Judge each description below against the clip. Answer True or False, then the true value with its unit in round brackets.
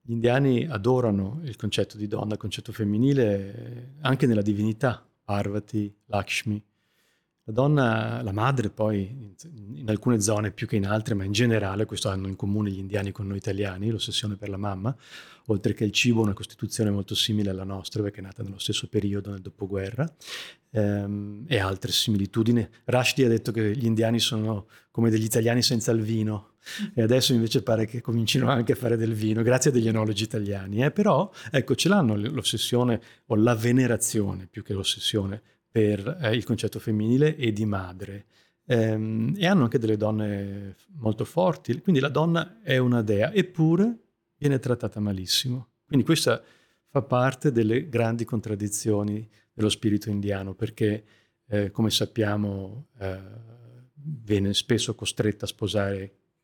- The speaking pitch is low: True (110 Hz)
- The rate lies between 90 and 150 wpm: False (160 wpm)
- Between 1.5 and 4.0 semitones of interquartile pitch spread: True (2.9 semitones)